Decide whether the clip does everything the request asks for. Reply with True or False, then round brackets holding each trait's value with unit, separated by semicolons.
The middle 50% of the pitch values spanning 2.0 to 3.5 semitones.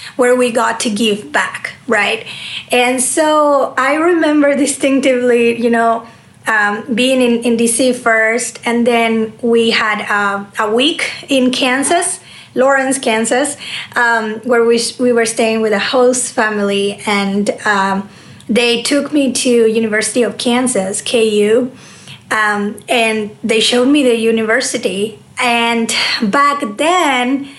True (2.6 semitones)